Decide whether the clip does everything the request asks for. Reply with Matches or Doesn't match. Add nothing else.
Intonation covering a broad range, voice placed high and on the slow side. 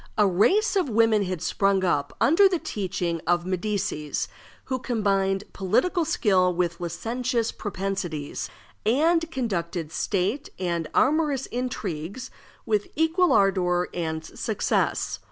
Matches